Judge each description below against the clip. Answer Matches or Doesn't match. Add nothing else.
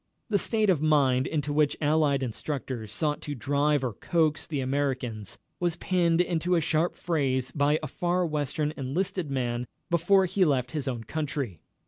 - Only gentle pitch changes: Doesn't match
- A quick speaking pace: Doesn't match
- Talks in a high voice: Doesn't match